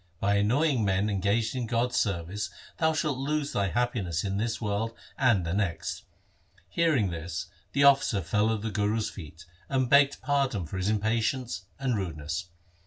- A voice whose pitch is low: Yes, low, 110 Hz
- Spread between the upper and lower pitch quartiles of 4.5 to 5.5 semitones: Yes, average, 4.9 semitones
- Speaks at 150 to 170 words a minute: Yes, average, 165 wpm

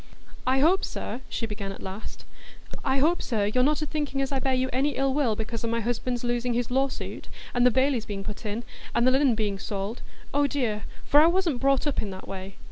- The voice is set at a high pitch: Yes, very high, 250 Hz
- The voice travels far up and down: No, average, 4.0 semitones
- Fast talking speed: Yes, fast, 215 wpm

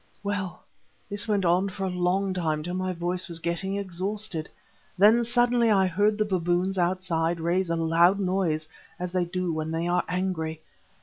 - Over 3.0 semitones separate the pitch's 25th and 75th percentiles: No, narrow, 2.4 semitones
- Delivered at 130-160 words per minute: No, average, 175 wpm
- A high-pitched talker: No, medium, 180 Hz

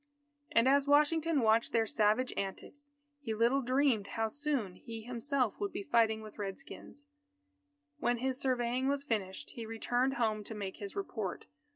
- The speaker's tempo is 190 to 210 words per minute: No, average, 165 wpm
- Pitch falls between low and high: No, high, 235 Hz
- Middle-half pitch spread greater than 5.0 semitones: No, average, 4.1 semitones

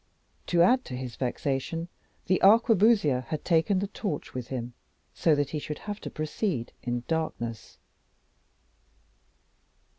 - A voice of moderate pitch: Yes, medium, 155 Hz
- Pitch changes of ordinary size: No, wide, 7.1 semitones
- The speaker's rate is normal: No, slow, 130 wpm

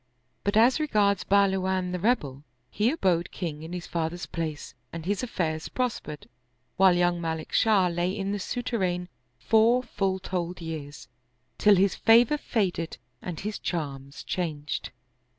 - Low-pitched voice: No, medium, 180 Hz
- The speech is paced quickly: No, average, 145 wpm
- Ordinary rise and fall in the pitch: Yes, average, 3.8 semitones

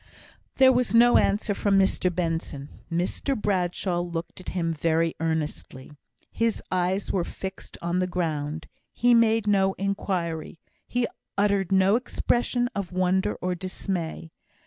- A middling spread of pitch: Yes, average, 3.4 semitones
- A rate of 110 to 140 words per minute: Yes, slow, 135 wpm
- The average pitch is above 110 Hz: Yes, medium, 185 Hz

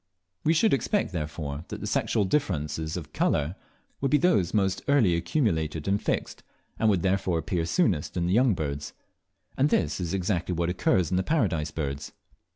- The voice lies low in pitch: Yes, very low, 90 Hz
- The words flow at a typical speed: Yes, average, 175 wpm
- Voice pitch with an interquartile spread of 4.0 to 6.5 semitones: Yes, average, 5.2 semitones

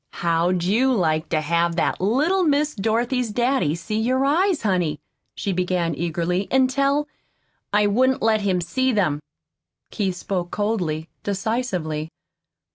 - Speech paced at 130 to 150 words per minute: Yes, average, 140 wpm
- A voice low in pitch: No, high, 200 Hz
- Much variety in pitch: Yes, wide, 6.9 semitones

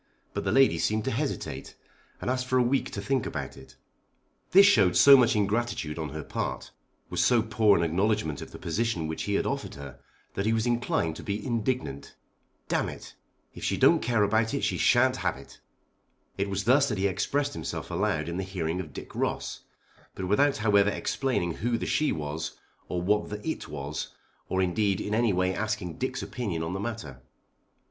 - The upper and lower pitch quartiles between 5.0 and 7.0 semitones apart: Yes, wide, 5.4 semitones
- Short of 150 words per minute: No, average, 200 wpm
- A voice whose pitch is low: Yes, low, 105 Hz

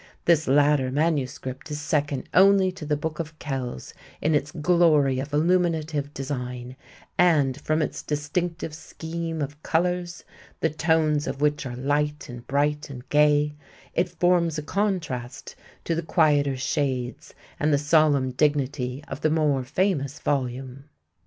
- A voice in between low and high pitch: Yes, medium, 150 Hz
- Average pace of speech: Yes, average, 145 wpm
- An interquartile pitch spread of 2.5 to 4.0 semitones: Yes, average, 2.9 semitones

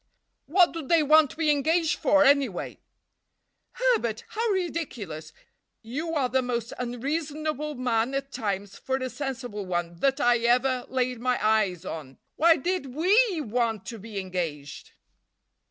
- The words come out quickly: No, average, 145 wpm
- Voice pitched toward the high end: Yes, very high, 255 Hz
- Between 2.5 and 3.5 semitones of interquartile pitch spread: No, wide, 5.6 semitones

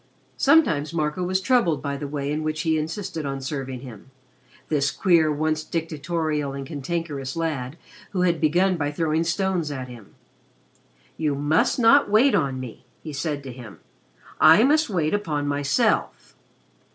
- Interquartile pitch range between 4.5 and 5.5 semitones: No, average, 3.4 semitones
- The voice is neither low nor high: Yes, medium, 155 Hz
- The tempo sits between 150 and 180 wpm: Yes, average, 155 wpm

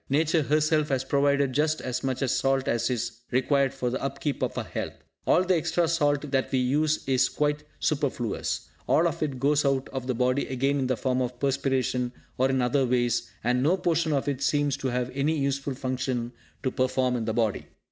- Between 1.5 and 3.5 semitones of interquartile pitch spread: Yes, narrow, 2.5 semitones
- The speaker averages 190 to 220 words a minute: Yes, fast, 205 wpm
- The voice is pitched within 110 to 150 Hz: Yes, low, 135 Hz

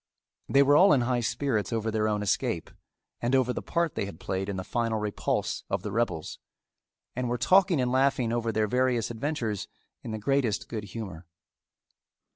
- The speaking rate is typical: Yes, average, 185 wpm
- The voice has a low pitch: Yes, low, 115 Hz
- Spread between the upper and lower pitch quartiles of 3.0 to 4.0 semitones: Yes, average, 3.4 semitones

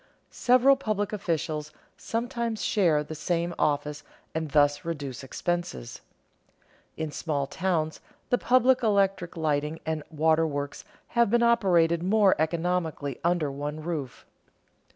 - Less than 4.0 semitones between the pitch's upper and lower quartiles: No, average, 5.1 semitones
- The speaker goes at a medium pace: No, slow, 115 wpm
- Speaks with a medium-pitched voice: Yes, medium, 165 Hz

